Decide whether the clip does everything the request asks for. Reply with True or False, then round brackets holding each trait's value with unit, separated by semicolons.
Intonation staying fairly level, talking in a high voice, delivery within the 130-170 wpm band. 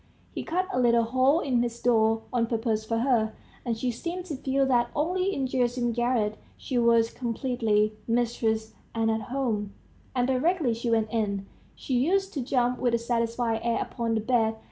False (2.3 semitones; 240 Hz; 185 wpm)